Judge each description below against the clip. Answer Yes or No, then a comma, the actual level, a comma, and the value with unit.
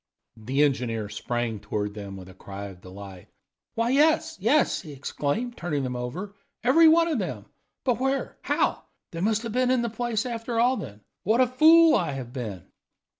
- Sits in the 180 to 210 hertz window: Yes, medium, 185 Hz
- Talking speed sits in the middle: Yes, average, 185 wpm